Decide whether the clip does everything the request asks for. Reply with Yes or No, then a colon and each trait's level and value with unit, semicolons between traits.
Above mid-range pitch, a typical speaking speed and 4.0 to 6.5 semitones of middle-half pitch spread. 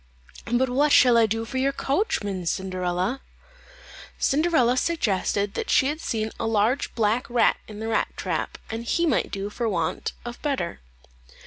Yes: high, 230 Hz; average, 160 wpm; average, 4.3 semitones